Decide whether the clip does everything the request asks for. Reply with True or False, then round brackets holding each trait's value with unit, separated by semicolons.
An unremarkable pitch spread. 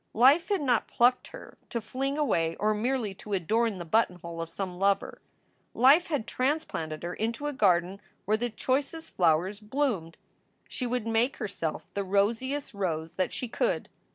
False (5.9 semitones)